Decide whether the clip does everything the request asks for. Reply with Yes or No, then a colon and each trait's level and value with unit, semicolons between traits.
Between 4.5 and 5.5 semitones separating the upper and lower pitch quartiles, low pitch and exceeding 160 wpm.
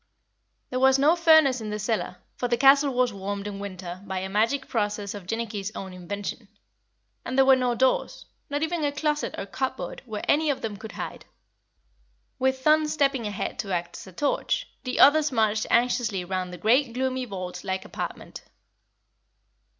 No: average, 5.1 semitones; high, 235 Hz; average, 180 wpm